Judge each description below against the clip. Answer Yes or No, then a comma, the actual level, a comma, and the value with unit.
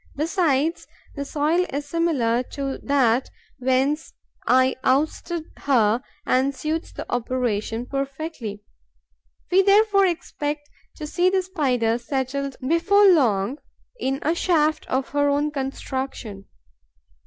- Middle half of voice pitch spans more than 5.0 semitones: No, average, 3.9 semitones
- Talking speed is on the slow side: Yes, slow, 115 wpm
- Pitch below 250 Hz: No, very high, 280 Hz